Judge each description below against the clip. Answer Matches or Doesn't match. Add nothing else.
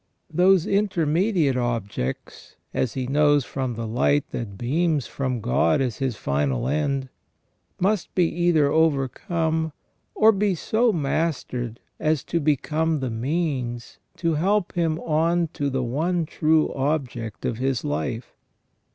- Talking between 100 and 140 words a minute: Matches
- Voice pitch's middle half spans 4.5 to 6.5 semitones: Matches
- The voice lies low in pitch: Doesn't match